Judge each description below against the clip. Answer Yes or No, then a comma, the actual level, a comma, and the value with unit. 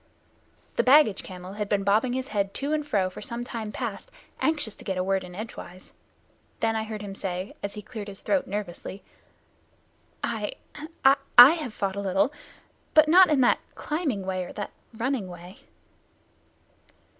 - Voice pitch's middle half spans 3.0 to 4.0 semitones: No, average, 4.9 semitones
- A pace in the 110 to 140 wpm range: No, average, 175 wpm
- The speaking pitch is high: Yes, high, 210 Hz